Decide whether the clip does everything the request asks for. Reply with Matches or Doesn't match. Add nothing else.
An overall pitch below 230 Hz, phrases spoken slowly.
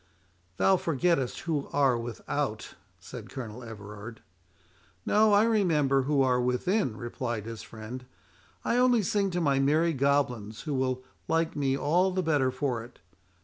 Doesn't match